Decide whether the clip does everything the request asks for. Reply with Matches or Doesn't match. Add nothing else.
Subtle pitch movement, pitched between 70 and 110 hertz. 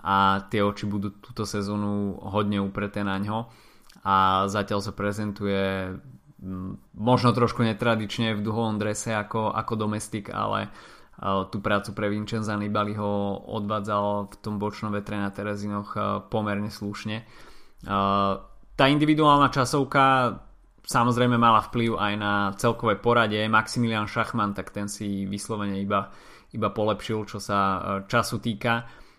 Matches